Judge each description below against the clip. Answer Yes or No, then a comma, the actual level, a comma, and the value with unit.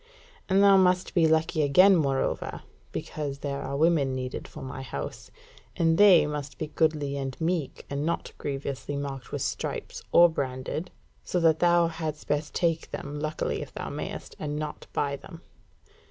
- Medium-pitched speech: Yes, medium, 150 Hz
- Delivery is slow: No, average, 170 wpm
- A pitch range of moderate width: Yes, average, 3.1 semitones